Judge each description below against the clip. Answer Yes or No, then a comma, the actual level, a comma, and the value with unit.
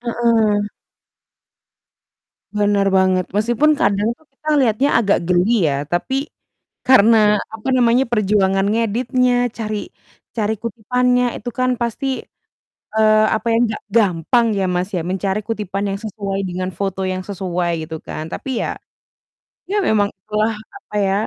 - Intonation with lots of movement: No, average, 3.3 semitones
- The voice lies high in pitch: Yes, high, 215 Hz